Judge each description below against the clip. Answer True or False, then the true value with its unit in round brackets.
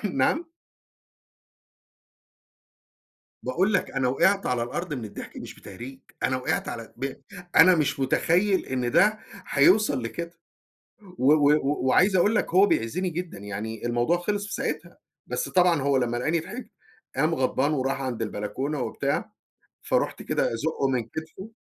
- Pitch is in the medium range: True (145 Hz)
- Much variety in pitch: True (6.2 semitones)